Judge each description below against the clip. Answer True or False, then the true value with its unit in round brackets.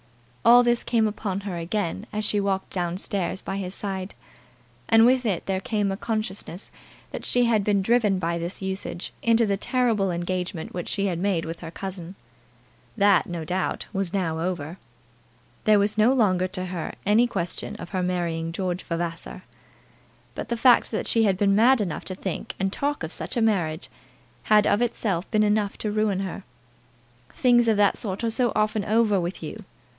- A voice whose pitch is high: True (195 Hz)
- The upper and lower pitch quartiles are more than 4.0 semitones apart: False (3.2 semitones)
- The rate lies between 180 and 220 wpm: True (190 wpm)